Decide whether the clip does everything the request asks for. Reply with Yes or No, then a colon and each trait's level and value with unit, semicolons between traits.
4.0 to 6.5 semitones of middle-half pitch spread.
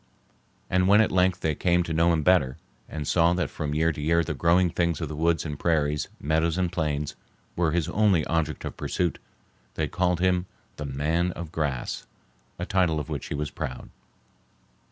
No: average, 2.7 semitones